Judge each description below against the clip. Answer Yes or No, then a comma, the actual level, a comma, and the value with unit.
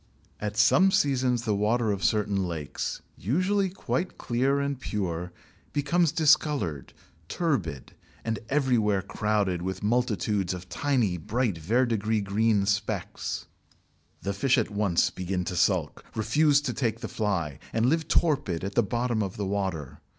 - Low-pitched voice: Yes, low, 105 Hz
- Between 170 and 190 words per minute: No, average, 145 wpm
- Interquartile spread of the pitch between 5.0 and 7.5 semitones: Yes, average, 5.3 semitones